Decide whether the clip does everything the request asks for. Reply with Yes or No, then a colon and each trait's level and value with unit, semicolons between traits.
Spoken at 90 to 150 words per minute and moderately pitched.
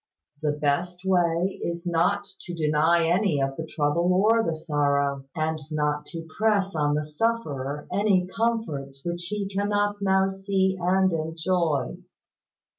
Yes: average, 140 wpm; medium, 170 Hz